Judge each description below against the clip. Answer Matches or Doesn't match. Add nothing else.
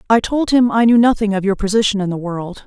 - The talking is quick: Matches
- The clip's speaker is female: Matches